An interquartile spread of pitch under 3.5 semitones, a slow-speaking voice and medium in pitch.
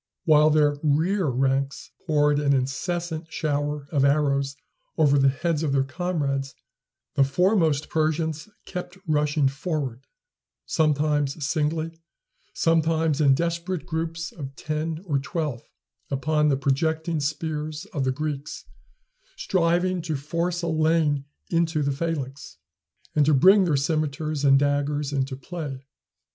Yes: average, 2.7 semitones; slow, 130 wpm; medium, 150 Hz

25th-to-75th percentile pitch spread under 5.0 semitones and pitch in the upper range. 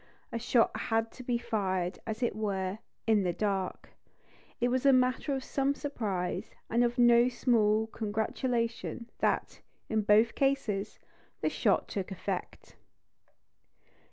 Yes: average, 2.9 semitones; high, 225 Hz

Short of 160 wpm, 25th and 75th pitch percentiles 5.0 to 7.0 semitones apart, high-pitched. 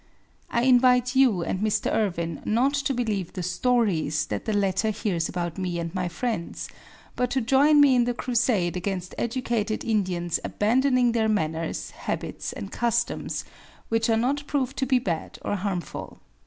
No: average, 165 wpm; wide, 5.5 semitones; high, 220 Hz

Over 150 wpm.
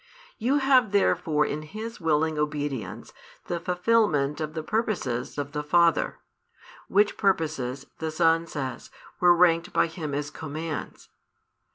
No: slow, 135 wpm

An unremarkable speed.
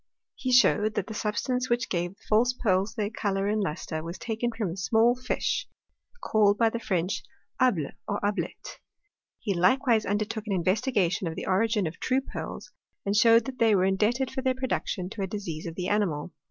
Yes: average, 195 wpm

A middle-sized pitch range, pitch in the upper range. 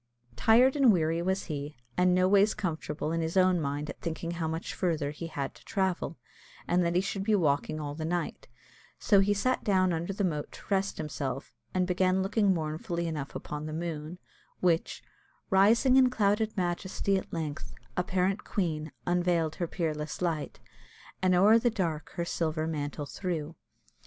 No: average, 3.5 semitones; medium, 175 Hz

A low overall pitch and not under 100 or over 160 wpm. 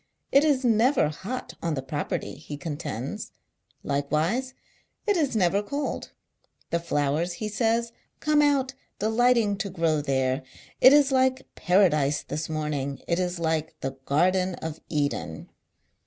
No: medium, 175 Hz; average, 140 wpm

